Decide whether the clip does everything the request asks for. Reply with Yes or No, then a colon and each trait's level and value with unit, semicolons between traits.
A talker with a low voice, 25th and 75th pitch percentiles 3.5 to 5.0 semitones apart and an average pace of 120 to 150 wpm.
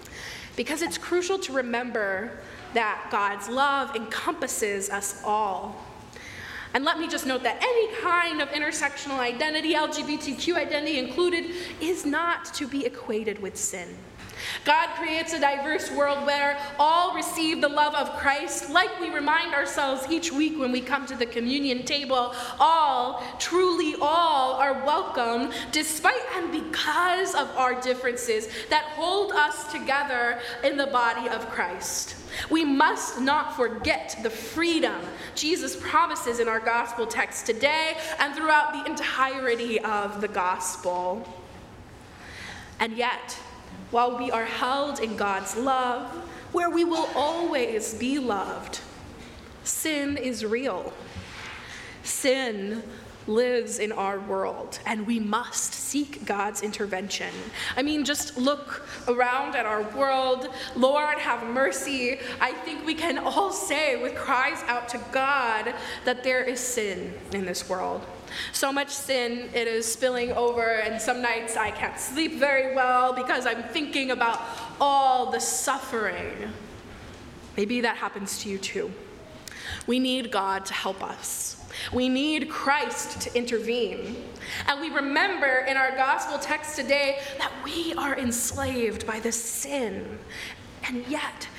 No: very high, 265 Hz; average, 4.2 semitones; average, 140 wpm